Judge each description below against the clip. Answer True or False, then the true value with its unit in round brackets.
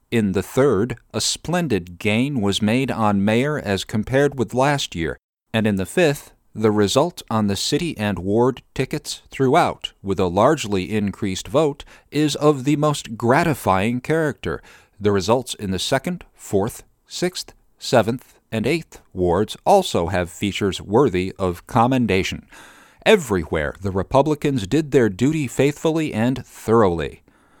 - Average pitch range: False (6.6 semitones)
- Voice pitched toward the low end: True (115 Hz)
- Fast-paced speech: False (140 wpm)